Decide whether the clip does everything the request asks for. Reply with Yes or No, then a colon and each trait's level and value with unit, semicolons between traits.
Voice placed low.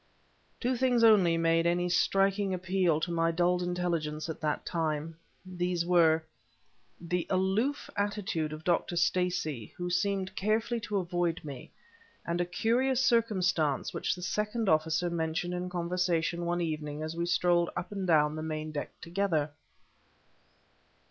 No: medium, 175 Hz